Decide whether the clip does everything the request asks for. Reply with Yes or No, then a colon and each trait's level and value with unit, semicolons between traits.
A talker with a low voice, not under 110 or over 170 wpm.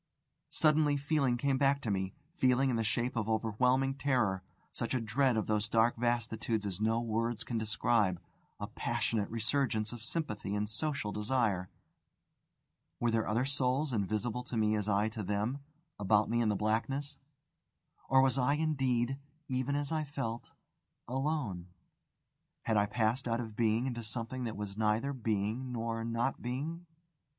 Yes: low, 115 Hz; average, 160 wpm